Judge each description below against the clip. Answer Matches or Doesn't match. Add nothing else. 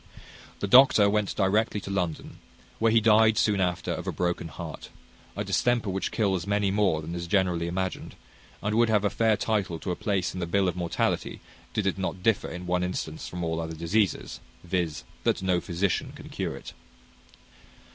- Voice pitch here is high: Doesn't match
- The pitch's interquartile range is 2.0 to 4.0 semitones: Matches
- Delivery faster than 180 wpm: Matches